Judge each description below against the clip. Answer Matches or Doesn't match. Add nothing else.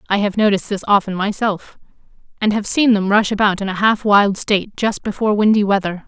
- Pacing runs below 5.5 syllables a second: Doesn't match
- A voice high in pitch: Matches